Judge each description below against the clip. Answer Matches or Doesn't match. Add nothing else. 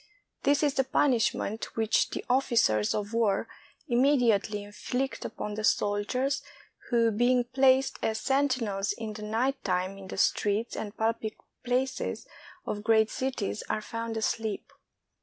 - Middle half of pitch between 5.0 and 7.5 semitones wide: Doesn't match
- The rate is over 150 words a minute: Doesn't match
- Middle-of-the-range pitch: Doesn't match